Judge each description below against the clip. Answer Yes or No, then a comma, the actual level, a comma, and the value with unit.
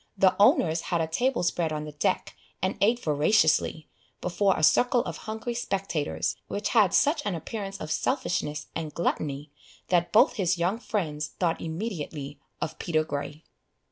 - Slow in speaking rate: No, average, 160 wpm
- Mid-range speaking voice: Yes, medium, 175 Hz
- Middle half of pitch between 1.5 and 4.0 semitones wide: No, average, 5.2 semitones